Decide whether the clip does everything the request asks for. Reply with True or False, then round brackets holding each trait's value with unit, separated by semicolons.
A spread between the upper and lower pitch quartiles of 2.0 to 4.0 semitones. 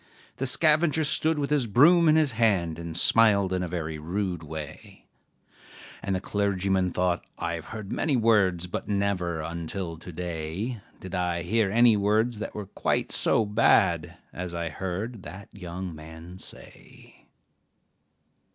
False (4.6 semitones)